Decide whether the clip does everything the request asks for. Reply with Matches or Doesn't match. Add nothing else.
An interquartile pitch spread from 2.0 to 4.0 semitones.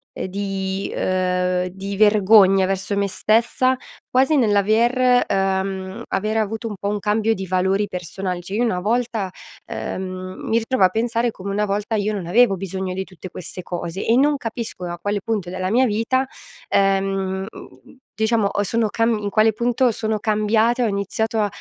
Matches